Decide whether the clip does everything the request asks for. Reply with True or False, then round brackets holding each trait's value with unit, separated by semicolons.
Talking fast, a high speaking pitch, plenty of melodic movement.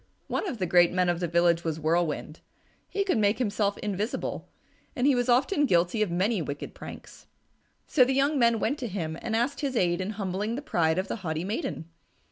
True (210 wpm; 200 Hz; 6.0 semitones)